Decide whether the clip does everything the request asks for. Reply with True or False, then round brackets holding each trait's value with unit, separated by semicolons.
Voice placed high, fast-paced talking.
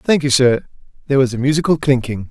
False (135 Hz; 210 wpm)